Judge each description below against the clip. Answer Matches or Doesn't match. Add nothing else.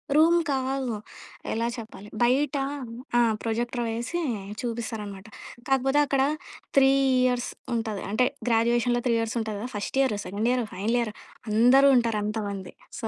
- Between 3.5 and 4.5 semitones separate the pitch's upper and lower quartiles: Doesn't match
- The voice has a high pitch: Matches